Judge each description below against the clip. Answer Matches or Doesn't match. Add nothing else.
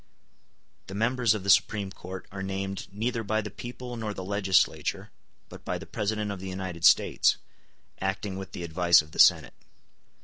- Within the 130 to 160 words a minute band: Doesn't match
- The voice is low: Matches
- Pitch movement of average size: Doesn't match